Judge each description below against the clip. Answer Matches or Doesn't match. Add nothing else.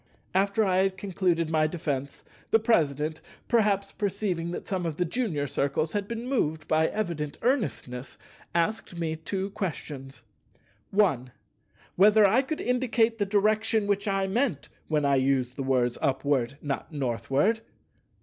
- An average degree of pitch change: Doesn't match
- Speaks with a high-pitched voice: Doesn't match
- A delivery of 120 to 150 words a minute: Matches